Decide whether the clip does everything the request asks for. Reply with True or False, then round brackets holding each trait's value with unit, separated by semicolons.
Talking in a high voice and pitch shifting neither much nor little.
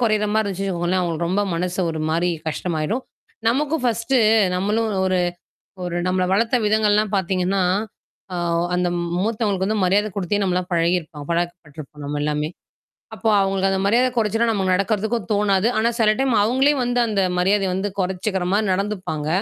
True (195 Hz; 3.3 semitones)